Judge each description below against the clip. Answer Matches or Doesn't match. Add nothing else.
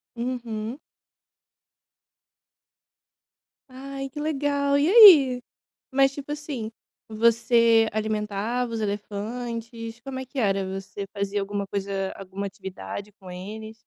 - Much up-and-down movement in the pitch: Doesn't match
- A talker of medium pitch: Doesn't match